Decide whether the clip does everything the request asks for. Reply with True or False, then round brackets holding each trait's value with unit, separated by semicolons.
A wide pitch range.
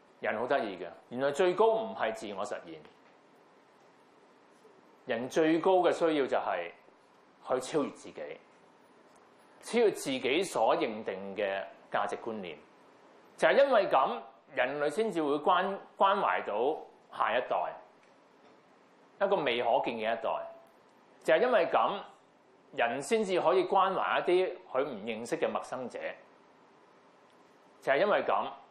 True (9.0 semitones)